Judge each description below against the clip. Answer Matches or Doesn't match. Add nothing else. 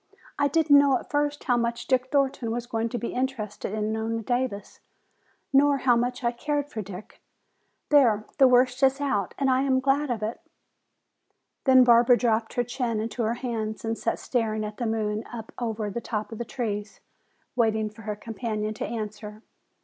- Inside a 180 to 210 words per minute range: Matches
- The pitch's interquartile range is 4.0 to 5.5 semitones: Doesn't match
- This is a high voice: Matches